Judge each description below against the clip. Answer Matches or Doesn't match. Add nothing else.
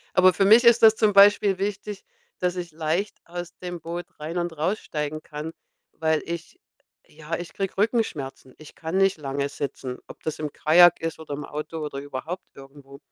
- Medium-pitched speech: Matches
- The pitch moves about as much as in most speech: Matches